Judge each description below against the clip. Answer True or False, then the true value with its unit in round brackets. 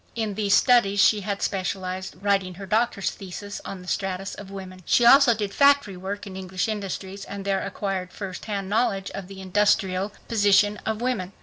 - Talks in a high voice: True (195 Hz)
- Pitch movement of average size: False (1.7 semitones)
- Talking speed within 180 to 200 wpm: True (185 wpm)